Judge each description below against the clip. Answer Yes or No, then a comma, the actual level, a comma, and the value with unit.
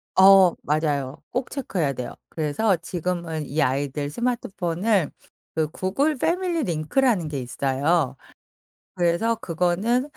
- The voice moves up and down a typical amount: No, wide, 6.9 semitones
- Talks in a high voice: No, medium, 175 Hz